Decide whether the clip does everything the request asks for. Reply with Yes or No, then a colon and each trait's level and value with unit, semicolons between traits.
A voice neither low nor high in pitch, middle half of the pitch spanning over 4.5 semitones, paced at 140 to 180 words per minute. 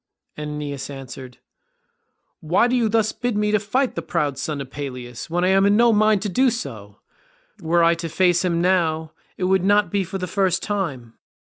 No: medium, 175 Hz; wide, 5.6 semitones; average, 200 wpm